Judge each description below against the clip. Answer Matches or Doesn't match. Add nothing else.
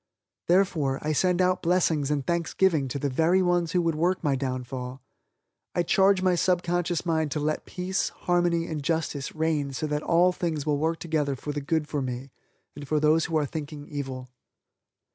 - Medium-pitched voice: Matches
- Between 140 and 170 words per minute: Doesn't match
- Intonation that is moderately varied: Matches